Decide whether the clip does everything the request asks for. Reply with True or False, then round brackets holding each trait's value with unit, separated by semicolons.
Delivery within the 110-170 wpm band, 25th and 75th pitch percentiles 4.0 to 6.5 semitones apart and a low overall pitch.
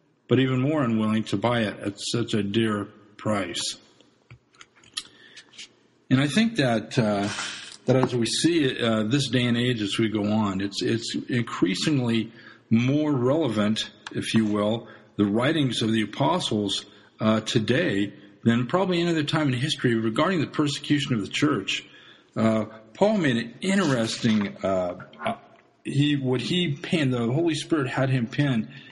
True (155 wpm; 4.9 semitones; 115 Hz)